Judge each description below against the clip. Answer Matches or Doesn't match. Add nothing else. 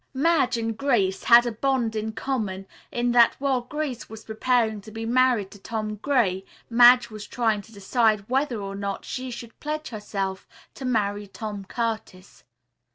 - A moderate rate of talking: Matches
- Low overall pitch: Doesn't match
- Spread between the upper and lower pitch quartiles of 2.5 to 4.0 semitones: Matches